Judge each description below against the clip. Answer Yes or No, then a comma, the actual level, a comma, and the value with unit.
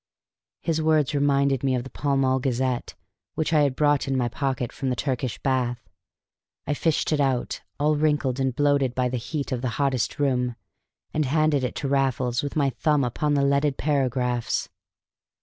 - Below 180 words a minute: No, average, 185 wpm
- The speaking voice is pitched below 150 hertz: Yes, low, 135 Hz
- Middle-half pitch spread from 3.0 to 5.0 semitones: No, narrow, 2.4 semitones